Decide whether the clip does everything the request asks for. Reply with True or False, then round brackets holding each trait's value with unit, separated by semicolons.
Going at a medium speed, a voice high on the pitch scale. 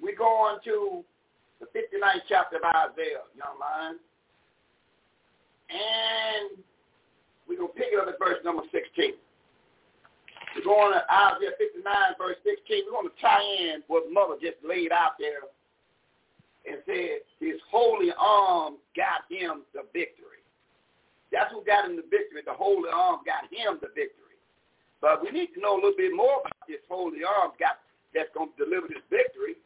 True (165 wpm; 370 Hz)